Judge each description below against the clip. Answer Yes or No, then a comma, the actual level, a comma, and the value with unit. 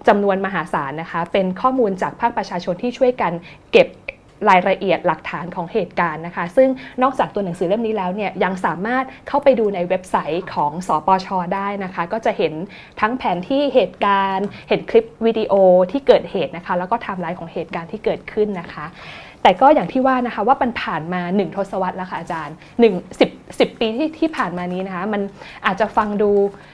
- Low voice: No, high, 200 Hz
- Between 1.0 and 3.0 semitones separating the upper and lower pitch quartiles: No, average, 4.2 semitones